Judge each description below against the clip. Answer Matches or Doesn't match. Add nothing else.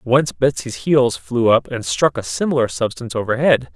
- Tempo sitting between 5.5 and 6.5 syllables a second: Doesn't match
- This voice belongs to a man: Matches